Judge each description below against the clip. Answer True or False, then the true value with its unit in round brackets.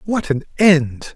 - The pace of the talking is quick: False (155 wpm)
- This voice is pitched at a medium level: True (160 Hz)